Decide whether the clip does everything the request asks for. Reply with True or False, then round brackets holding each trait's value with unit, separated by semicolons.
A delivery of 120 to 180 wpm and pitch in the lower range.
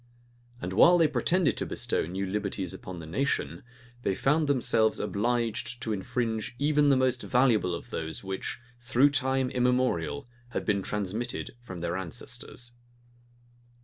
True (145 wpm; 120 Hz)